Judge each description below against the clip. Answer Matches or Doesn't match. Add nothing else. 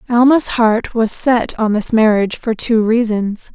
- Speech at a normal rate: Matches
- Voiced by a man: Doesn't match